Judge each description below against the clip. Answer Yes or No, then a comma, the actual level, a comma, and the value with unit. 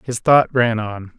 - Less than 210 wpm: Yes, average, 200 wpm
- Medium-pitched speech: No, low, 115 Hz